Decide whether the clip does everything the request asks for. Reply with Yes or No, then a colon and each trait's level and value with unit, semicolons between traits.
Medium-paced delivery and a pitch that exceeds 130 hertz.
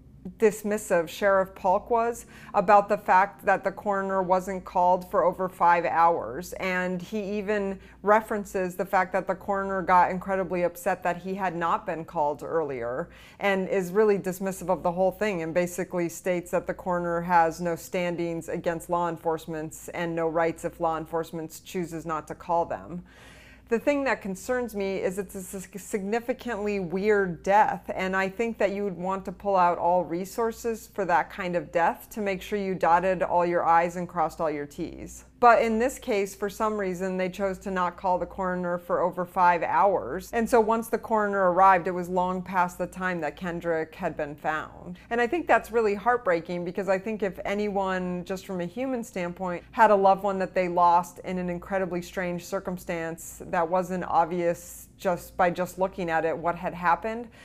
Yes: average, 190 wpm; medium, 185 Hz